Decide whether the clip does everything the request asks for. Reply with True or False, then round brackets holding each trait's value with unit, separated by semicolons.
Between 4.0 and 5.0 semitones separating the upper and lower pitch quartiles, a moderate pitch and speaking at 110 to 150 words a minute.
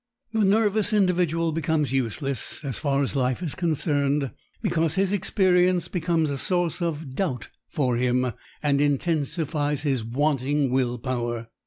True (4.5 semitones; 150 Hz; 140 wpm)